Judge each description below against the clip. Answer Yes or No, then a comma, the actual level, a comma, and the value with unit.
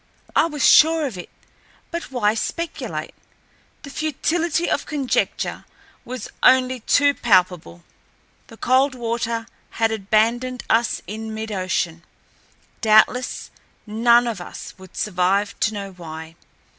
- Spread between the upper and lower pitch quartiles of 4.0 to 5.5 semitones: Yes, average, 4.4 semitones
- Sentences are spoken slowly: Yes, slow, 115 wpm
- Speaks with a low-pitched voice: No, high, 230 Hz